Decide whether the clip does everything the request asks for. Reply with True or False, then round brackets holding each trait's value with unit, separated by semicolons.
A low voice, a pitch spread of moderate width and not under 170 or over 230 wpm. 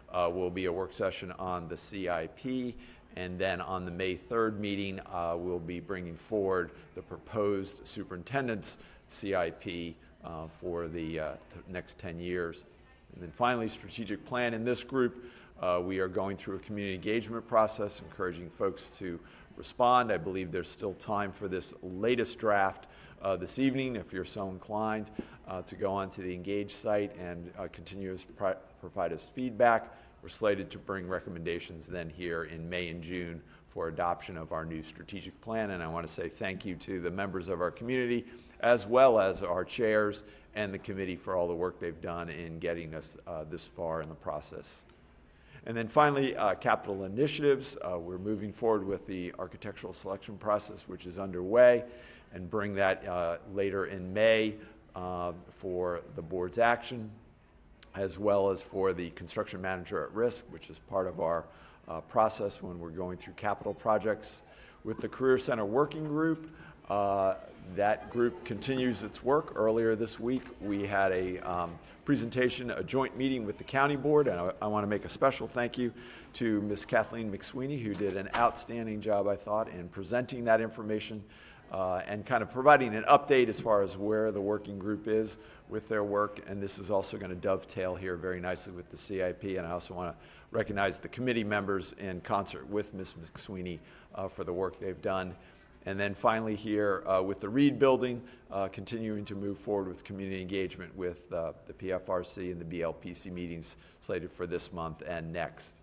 True (100 Hz; 3.8 semitones; 185 wpm)